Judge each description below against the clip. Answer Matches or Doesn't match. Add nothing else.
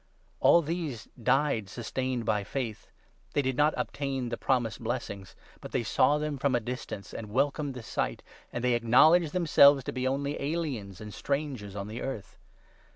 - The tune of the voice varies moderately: Matches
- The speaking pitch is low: Matches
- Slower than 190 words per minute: Matches